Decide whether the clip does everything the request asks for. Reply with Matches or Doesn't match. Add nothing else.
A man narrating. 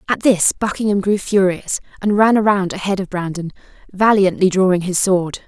Doesn't match